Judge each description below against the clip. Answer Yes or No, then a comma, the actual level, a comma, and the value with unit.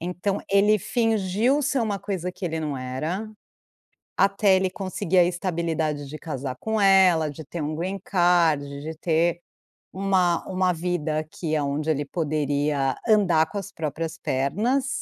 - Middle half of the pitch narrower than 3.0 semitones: No, average, 4.1 semitones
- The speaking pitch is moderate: Yes, medium, 175 Hz